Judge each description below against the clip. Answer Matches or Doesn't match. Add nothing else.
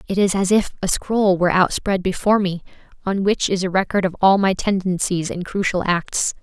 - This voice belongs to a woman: Matches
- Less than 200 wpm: Doesn't match